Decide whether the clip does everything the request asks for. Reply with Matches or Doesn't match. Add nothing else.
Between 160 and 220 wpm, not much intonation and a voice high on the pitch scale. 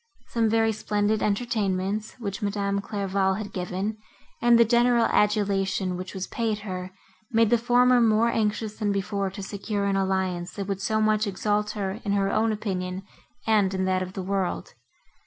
Matches